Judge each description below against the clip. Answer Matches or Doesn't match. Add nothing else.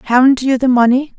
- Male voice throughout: Doesn't match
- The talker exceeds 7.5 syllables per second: Doesn't match